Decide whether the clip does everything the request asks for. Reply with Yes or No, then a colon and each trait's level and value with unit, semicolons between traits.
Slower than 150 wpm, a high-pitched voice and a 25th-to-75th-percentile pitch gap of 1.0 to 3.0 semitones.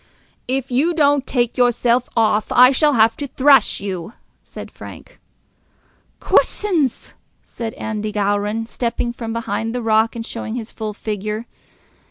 Yes: average, 140 wpm; high, 230 Hz; average, 2.7 semitones